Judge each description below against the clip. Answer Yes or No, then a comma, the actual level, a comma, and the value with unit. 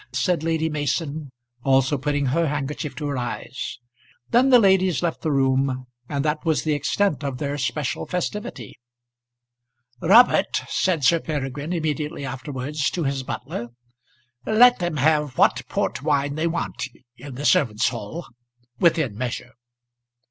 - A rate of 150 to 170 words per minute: No, average, 140 wpm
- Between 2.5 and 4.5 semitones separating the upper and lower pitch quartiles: Yes, average, 3.6 semitones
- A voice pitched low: No, medium, 145 Hz